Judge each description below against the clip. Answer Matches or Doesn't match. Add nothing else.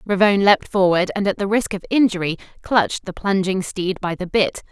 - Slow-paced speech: Doesn't match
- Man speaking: Doesn't match